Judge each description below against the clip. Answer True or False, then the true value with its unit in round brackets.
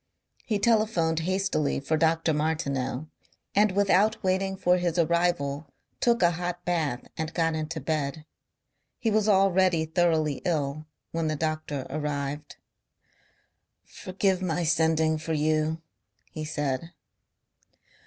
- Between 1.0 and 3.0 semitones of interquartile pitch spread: True (2.7 semitones)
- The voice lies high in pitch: False (160 Hz)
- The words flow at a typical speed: False (120 wpm)